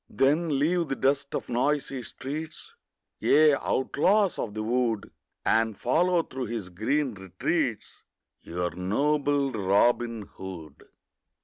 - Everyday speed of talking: No, slow, 115 wpm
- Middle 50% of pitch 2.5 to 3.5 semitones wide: No, wide, 5.6 semitones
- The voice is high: No, low, 130 Hz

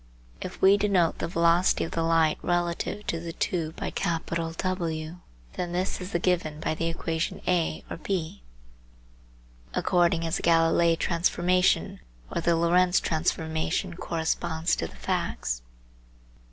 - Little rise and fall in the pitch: Yes, narrow, 1.6 semitones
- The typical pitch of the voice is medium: Yes, medium, 170 Hz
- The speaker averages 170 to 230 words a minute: No, slow, 135 wpm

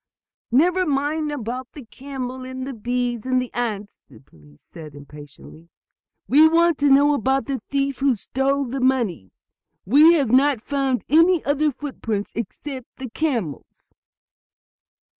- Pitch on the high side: Yes, very high, 260 Hz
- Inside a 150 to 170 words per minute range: No, average, 140 wpm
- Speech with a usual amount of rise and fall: Yes, average, 3.9 semitones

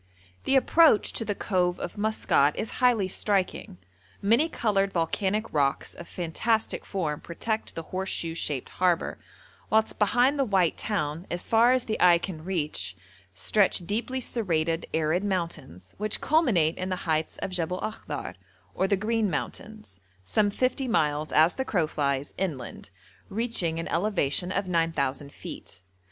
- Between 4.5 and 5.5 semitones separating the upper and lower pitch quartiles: Yes, average, 5.1 semitones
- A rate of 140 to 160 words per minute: Yes, average, 150 wpm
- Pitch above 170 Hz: Yes, medium, 185 Hz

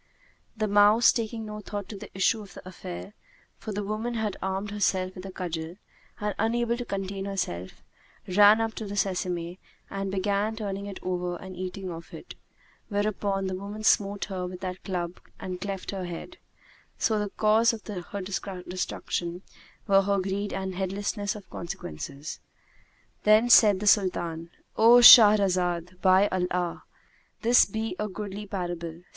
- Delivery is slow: No, average, 160 wpm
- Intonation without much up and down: Yes, narrow, 2.3 semitones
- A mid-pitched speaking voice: No, high, 195 Hz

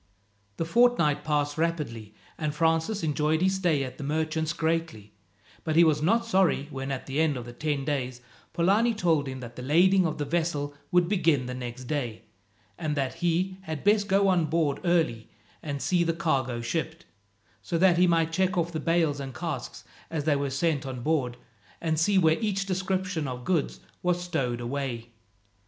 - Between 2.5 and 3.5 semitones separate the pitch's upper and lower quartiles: No, average, 4.0 semitones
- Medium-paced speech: Yes, average, 185 wpm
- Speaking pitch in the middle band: Yes, medium, 160 Hz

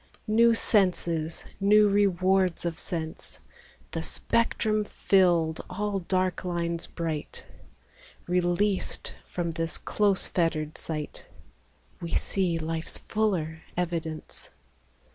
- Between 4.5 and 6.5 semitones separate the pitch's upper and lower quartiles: No, average, 3.1 semitones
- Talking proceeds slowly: Yes, slow, 95 wpm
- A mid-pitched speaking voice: Yes, medium, 175 Hz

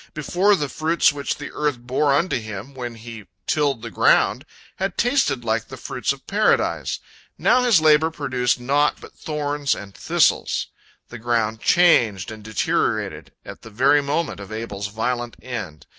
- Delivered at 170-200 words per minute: No, average, 160 wpm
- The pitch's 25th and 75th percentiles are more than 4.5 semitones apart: Yes, average, 5.0 semitones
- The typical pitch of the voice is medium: No, low, 130 Hz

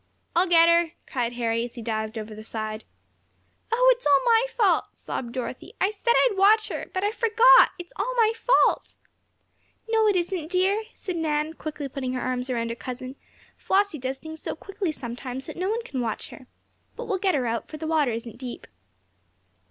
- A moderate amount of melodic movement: No, wide, 8.3 semitones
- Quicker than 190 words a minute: Yes, average, 200 wpm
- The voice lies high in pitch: Yes, very high, 315 Hz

